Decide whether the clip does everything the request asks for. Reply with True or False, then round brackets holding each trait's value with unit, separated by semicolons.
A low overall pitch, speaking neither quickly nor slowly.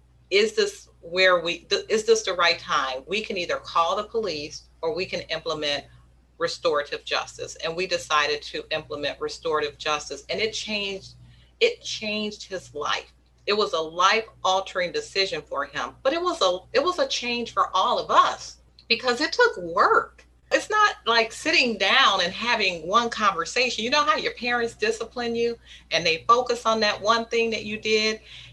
False (220 Hz; 180 wpm)